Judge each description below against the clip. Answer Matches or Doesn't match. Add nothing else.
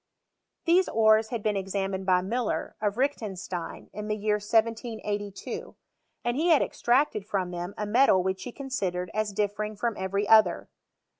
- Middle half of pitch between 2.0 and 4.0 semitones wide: Matches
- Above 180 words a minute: Doesn't match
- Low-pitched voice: Doesn't match